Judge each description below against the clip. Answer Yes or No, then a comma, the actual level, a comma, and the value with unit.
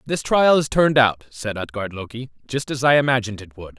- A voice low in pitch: Yes, low, 125 Hz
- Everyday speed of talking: No, fast, 220 wpm